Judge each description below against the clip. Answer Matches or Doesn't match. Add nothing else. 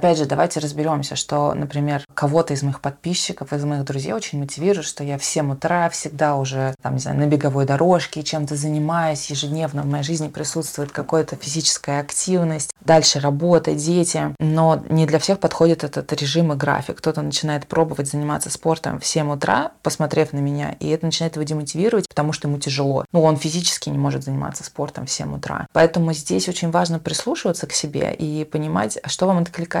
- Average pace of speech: Doesn't match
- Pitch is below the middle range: Doesn't match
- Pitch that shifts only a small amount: Matches